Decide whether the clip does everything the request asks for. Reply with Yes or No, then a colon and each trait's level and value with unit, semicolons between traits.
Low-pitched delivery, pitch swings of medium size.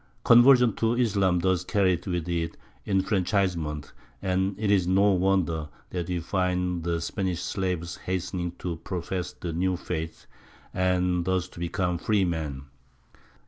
No: very low, 90 Hz; narrow, 1.9 semitones